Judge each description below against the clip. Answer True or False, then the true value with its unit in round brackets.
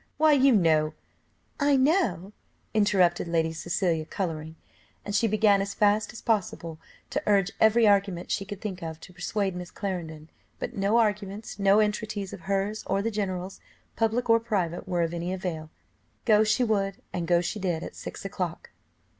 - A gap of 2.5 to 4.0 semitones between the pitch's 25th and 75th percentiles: True (3.5 semitones)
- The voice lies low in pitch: False (195 Hz)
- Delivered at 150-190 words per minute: True (175 wpm)